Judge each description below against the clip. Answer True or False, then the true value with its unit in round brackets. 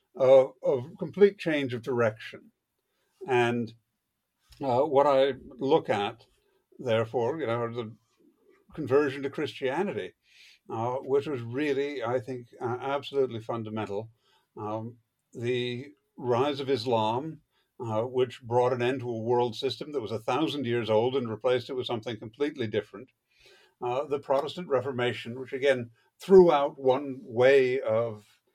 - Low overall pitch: True (130 Hz)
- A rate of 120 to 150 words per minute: True (140 wpm)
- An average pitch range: True (3.0 semitones)